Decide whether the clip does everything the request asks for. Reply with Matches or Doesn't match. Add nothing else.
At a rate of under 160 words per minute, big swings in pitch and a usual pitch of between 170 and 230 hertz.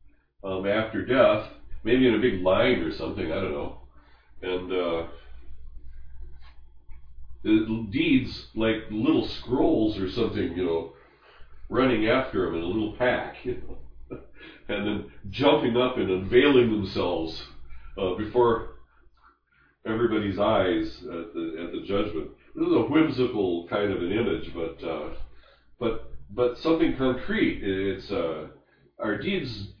Doesn't match